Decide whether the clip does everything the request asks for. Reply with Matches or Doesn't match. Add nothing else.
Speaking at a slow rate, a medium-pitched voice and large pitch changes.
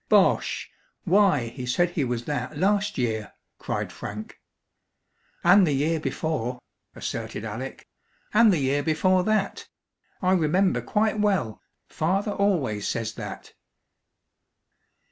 Matches